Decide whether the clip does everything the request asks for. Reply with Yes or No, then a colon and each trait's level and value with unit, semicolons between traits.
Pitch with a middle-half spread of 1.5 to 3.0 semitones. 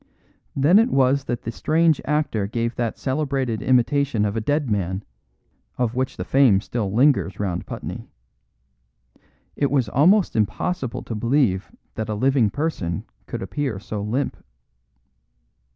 No: average, 5.1 semitones